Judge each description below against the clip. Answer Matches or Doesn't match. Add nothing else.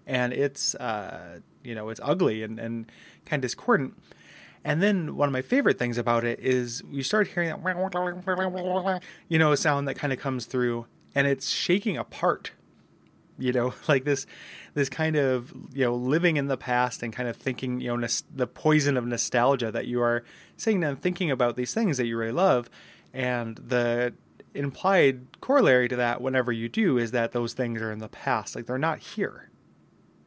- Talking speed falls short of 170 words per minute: Doesn't match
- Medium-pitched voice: Doesn't match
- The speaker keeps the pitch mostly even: Doesn't match